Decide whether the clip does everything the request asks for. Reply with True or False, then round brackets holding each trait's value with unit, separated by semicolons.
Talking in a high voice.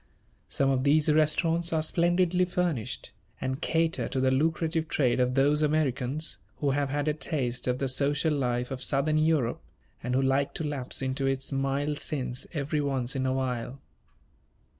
False (140 Hz)